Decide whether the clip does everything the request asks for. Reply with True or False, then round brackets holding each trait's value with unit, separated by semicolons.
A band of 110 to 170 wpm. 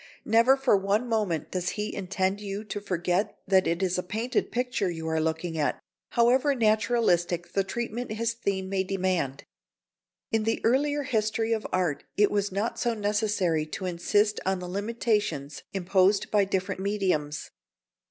True (160 wpm)